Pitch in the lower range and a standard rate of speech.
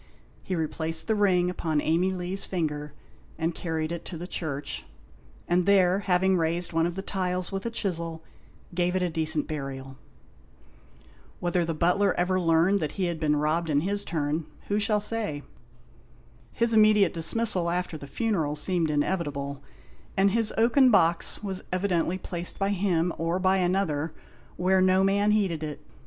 No: medium, 175 Hz; average, 160 wpm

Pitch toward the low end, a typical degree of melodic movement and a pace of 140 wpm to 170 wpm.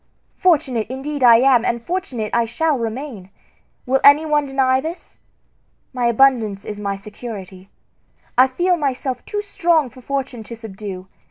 No: very high, 255 Hz; average, 4.3 semitones; average, 150 wpm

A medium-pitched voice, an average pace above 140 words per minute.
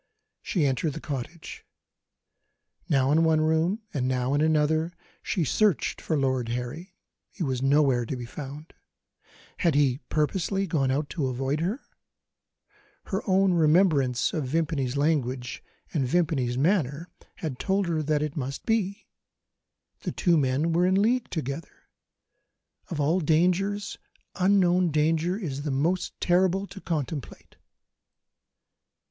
No: medium, 155 Hz; slow, 135 wpm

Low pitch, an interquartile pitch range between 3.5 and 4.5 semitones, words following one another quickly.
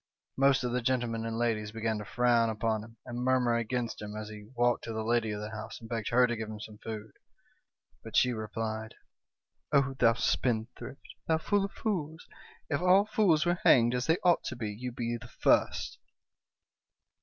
No: low, 115 Hz; average, 2.8 semitones; fast, 210 wpm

